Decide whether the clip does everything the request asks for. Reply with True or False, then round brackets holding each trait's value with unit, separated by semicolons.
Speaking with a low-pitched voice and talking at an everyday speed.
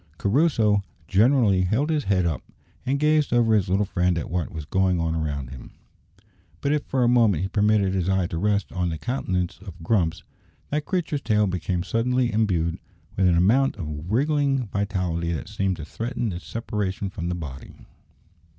True (100 Hz; 180 wpm)